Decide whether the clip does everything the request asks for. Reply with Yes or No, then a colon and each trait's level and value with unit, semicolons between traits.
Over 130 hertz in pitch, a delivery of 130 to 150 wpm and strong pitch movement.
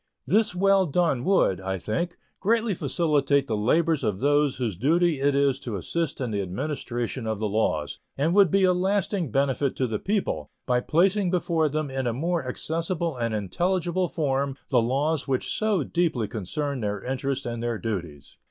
No: medium, 140 Hz; average, 180 wpm; wide, 6.6 semitones